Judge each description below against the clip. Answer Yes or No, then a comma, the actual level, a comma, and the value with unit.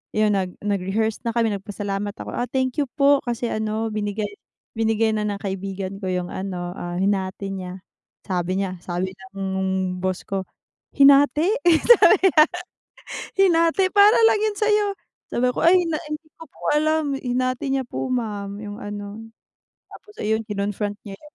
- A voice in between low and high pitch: No, high, 215 Hz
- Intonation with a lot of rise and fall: Yes, wide, 6.0 semitones